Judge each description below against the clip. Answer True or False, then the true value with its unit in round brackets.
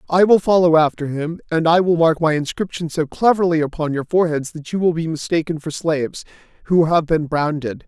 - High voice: False (160 Hz)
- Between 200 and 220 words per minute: True (205 wpm)